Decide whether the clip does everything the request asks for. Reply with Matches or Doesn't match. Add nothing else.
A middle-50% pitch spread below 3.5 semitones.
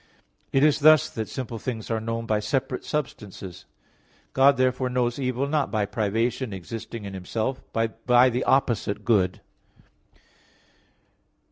Matches